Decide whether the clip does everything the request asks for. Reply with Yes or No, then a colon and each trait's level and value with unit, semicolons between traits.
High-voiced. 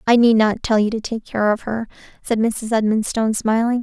Yes: high, 220 Hz